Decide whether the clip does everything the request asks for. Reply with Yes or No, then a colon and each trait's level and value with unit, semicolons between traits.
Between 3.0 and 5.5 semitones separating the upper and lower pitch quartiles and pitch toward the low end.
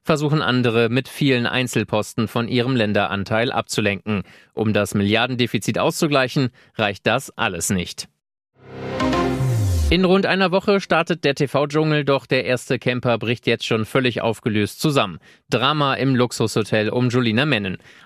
Yes: average, 3.9 semitones; low, 125 Hz